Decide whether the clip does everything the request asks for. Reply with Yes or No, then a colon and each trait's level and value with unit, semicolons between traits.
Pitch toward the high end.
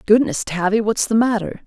Yes: high, 215 Hz